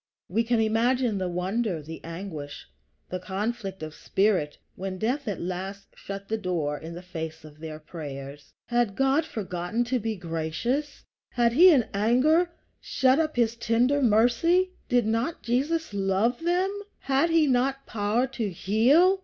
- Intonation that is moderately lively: No, wide, 6.3 semitones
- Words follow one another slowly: No, average, 155 wpm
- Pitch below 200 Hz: No, high, 220 Hz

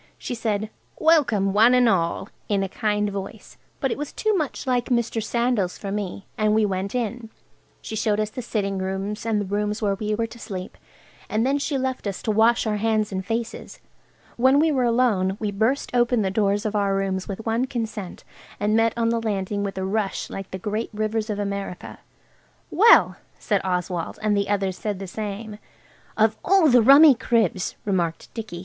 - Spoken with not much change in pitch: No, average, 3.0 semitones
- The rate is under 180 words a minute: No, average, 195 wpm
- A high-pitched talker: Yes, high, 215 Hz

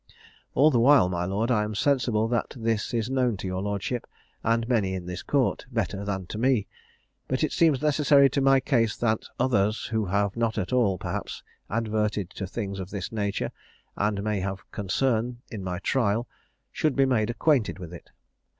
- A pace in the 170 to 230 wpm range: Yes, average, 185 wpm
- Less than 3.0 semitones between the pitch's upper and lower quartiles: No, average, 4.2 semitones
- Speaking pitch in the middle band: No, low, 110 Hz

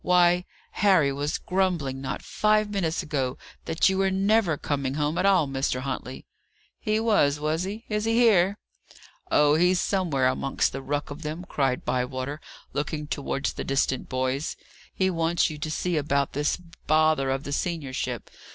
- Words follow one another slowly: No, average, 165 wpm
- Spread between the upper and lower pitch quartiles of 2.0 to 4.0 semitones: No, average, 5.1 semitones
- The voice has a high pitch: No, medium, 155 Hz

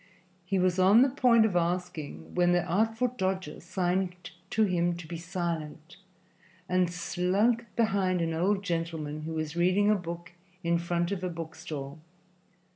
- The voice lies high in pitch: No, medium, 180 Hz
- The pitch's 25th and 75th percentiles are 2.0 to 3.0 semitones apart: Yes, narrow, 2.4 semitones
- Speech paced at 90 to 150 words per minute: No, average, 160 wpm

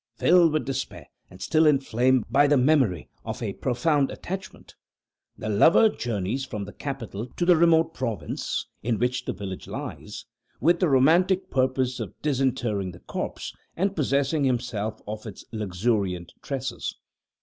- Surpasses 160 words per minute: No, average, 150 wpm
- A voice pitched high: No, low, 130 Hz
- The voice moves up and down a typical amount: No, wide, 6.0 semitones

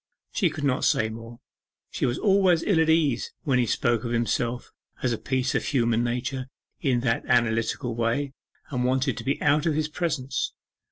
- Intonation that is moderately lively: Yes, average, 3.7 semitones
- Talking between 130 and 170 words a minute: No, average, 185 wpm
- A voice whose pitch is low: Yes, low, 130 Hz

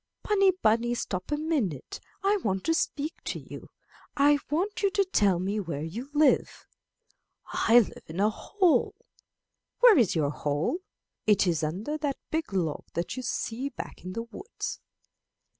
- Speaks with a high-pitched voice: Yes, high, 235 Hz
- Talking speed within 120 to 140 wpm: No, average, 160 wpm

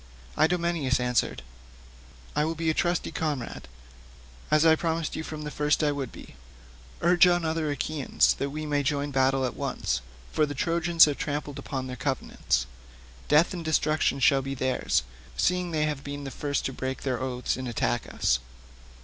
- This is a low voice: No, medium, 145 Hz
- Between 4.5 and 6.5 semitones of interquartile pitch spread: No, average, 3.1 semitones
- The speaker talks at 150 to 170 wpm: No, average, 185 wpm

